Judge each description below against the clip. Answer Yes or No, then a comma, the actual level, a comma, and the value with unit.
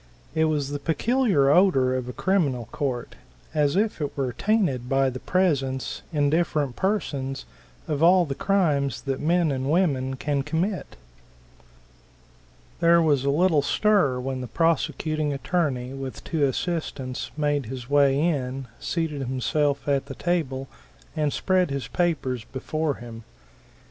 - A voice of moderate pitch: Yes, medium, 145 Hz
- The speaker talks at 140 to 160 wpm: Yes, average, 145 wpm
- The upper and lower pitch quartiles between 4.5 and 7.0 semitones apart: No, average, 3.9 semitones